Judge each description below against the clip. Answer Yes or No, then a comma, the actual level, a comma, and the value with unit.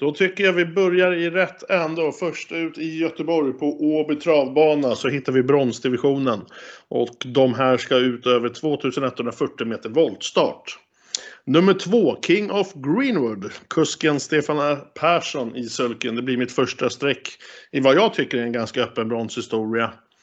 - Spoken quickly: No, average, 155 wpm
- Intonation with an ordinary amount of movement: Yes, average, 4.5 semitones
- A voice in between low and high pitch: Yes, medium, 145 Hz